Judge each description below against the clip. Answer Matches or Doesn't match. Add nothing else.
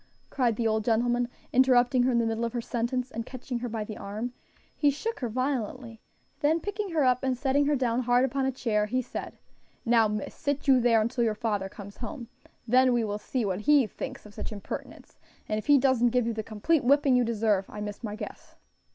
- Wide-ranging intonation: Doesn't match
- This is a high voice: Matches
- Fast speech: Matches